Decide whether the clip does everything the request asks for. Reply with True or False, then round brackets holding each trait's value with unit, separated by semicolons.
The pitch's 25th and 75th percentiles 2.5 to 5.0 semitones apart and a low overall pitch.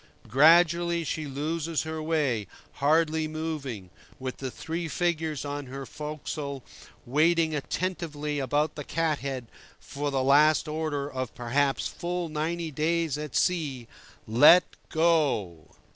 False (2.9 semitones; 150 Hz)